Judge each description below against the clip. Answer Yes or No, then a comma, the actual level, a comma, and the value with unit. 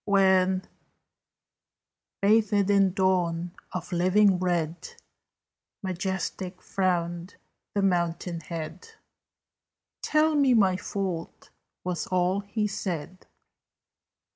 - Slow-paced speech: Yes, slow, 85 wpm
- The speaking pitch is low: No, medium, 185 Hz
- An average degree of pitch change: No, narrow, 2.3 semitones